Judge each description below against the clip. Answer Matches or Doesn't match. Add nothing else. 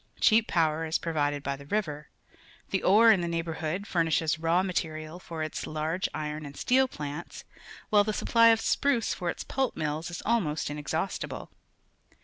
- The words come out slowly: Doesn't match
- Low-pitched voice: Doesn't match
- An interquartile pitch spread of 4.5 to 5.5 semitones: Matches